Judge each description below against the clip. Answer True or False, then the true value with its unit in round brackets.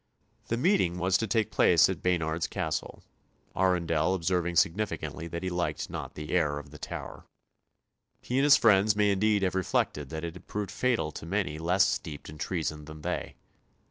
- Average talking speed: True (180 wpm)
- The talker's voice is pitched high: False (90 Hz)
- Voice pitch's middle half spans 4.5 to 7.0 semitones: False (3.9 semitones)